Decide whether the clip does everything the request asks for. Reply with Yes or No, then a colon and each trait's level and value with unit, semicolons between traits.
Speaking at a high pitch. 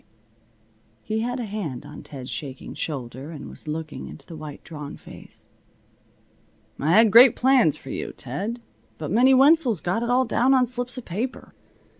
Yes: high, 210 Hz